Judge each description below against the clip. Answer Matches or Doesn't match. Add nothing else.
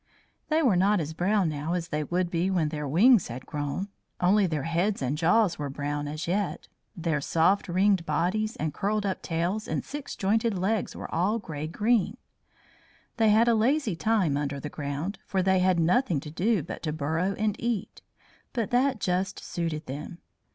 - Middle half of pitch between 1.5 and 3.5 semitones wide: Doesn't match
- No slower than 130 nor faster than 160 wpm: Doesn't match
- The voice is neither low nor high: Matches